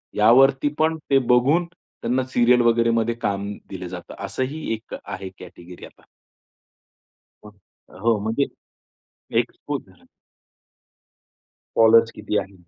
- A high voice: No, low, 115 Hz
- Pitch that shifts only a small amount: No, average, 3.9 semitones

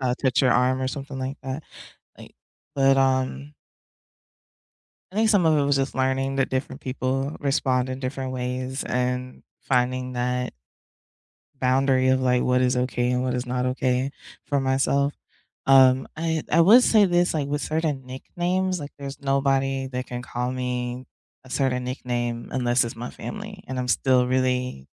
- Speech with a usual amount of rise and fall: No, narrow, 1.6 semitones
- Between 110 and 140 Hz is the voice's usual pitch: Yes, low, 130 Hz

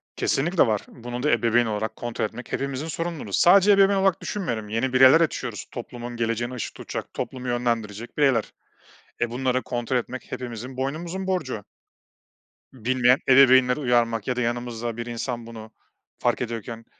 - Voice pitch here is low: Yes, low, 120 Hz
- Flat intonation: Yes, narrow, 2.3 semitones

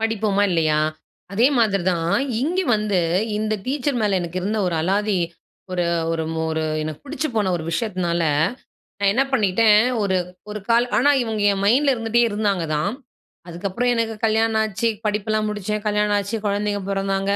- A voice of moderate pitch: No, high, 210 Hz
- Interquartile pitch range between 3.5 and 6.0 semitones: No, average, 2.8 semitones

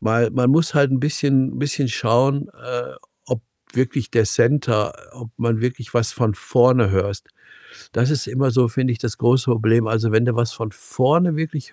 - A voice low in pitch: Yes, low, 120 Hz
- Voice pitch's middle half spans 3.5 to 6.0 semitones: No, average, 2.7 semitones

